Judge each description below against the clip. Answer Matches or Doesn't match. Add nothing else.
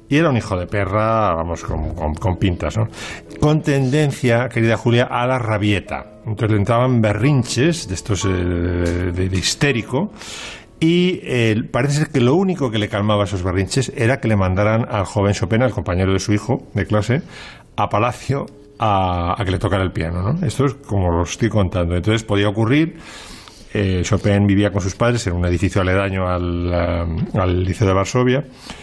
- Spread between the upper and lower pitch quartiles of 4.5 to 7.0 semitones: Matches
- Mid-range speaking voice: Doesn't match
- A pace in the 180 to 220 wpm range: Matches